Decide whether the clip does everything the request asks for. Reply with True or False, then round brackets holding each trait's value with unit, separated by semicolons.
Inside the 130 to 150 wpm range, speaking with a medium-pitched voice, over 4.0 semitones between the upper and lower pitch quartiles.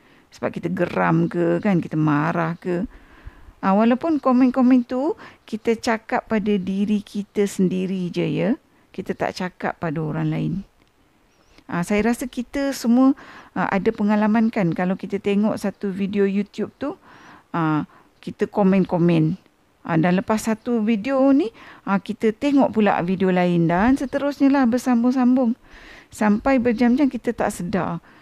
False (140 wpm; 210 Hz; 5.2 semitones)